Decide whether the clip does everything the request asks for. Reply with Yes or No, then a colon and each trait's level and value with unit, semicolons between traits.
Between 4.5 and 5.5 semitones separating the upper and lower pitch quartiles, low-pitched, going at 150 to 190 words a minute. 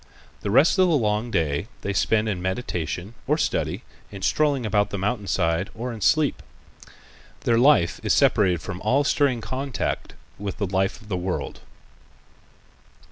Yes: average, 5.2 semitones; low, 105 Hz; average, 160 wpm